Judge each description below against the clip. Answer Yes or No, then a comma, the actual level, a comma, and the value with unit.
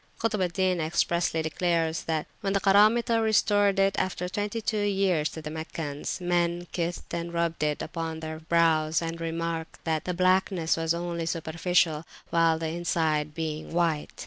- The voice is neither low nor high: Yes, medium, 170 Hz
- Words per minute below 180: Yes, average, 165 wpm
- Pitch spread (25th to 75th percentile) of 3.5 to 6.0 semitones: No, narrow, 2.4 semitones